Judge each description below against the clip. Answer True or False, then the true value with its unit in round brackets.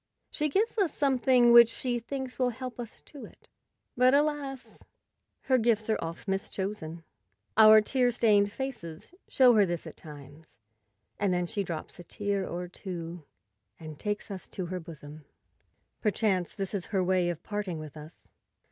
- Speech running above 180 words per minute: False (165 wpm)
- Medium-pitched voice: False (205 Hz)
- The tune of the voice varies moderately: False (6.0 semitones)